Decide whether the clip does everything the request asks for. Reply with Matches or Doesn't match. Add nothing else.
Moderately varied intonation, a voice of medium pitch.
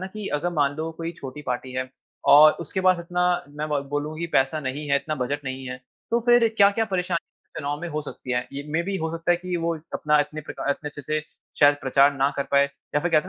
Matches